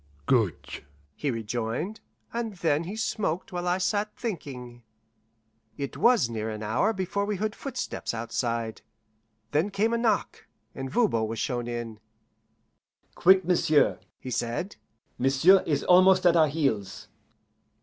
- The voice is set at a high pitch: No, medium, 155 Hz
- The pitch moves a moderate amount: No, wide, 8.6 semitones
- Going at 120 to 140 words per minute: Yes, slow, 135 wpm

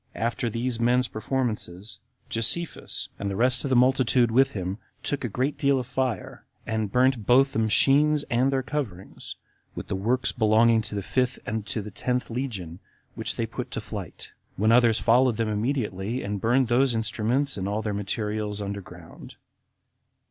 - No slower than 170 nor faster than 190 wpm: Yes, average, 175 wpm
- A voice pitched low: Yes, low, 115 Hz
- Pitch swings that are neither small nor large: Yes, average, 3.5 semitones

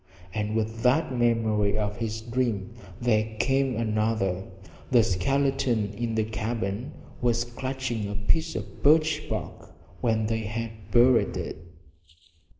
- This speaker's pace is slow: Yes, slow, 130 wpm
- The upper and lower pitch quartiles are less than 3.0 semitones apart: Yes, narrow, 2.4 semitones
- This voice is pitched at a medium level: No, low, 115 Hz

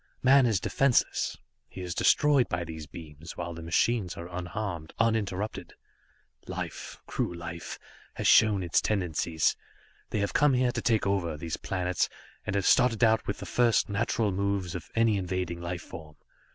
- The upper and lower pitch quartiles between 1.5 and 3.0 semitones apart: No, average, 4.6 semitones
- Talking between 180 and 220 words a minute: No, average, 165 wpm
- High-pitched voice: No, very low, 95 Hz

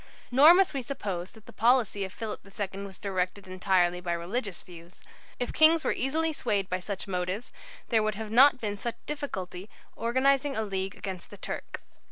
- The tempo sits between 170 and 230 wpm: Yes, average, 190 wpm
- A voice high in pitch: Yes, high, 205 Hz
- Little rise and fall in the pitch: No, average, 5.2 semitones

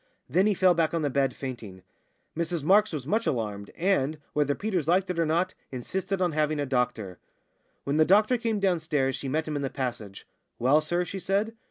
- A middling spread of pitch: No, wide, 5.7 semitones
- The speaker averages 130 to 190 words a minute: No, fast, 205 wpm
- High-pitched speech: No, medium, 155 Hz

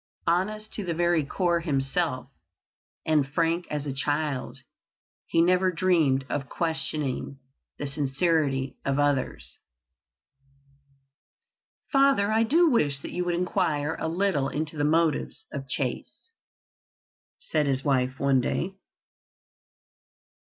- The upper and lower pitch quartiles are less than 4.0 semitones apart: No, average, 4.3 semitones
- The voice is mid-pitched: Yes, medium, 155 Hz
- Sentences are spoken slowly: Yes, slow, 115 wpm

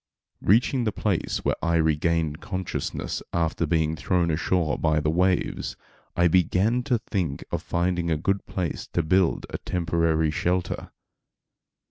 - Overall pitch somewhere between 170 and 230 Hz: No, very low, 85 Hz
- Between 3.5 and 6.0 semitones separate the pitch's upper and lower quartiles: No, narrow, 2.5 semitones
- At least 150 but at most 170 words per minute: No, average, 140 wpm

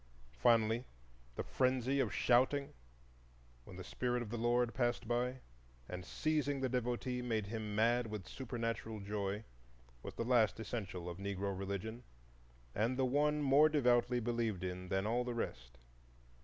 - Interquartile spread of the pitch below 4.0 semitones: Yes, average, 3.3 semitones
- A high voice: No, low, 120 Hz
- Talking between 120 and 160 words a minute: Yes, average, 150 wpm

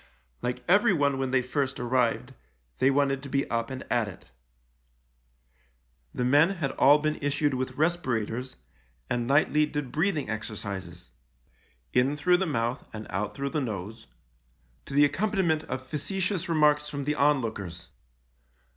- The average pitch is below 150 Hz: Yes, low, 135 Hz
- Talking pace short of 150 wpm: No, average, 155 wpm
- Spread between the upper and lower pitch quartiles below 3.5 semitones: No, average, 4.3 semitones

